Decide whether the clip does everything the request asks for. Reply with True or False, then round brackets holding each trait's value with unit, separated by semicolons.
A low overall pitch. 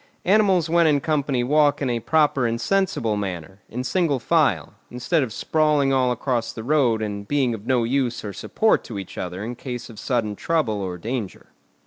True (125 Hz)